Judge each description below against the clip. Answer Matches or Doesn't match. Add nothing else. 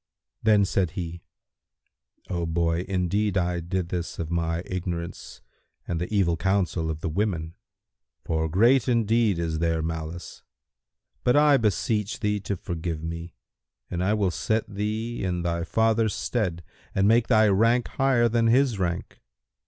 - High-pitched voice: Doesn't match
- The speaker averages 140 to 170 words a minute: Matches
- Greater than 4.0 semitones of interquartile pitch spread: Matches